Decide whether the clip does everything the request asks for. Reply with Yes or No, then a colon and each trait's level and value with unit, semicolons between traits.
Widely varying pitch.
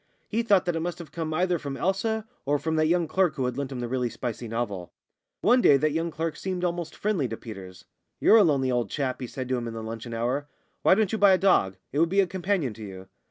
Yes: wide, 6.9 semitones